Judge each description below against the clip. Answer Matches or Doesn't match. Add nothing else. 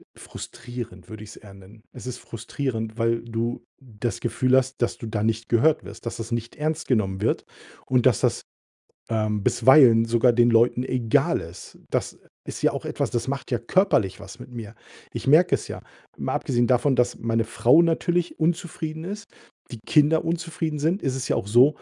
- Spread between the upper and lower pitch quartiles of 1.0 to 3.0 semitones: Doesn't match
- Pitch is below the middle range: Matches